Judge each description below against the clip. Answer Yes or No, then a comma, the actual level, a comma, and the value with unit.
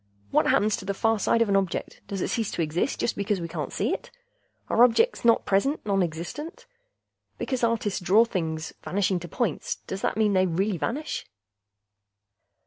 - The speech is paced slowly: No, average, 185 wpm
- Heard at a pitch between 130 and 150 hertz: No, high, 200 Hz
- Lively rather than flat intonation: No, average, 4.1 semitones